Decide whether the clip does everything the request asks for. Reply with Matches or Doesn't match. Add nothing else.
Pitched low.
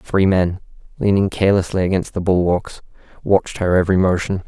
Matches